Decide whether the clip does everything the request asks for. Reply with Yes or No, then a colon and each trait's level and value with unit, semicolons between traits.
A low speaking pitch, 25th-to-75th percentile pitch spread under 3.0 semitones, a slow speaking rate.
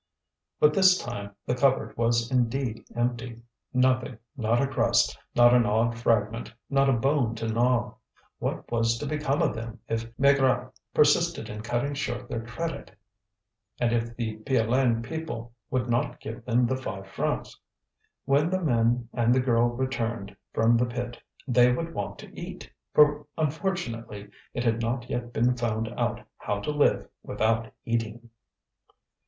No: low, 120 Hz; narrow, 2.4 semitones; average, 155 wpm